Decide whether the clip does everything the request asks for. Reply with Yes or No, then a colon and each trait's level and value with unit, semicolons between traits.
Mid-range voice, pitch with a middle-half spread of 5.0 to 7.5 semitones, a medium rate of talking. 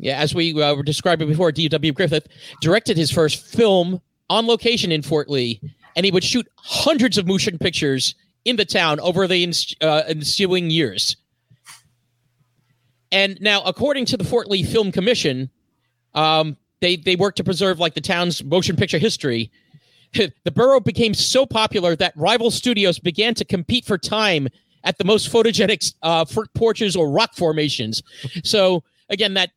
Yes: medium, 175 Hz; wide, 5.6 semitones; average, 165 wpm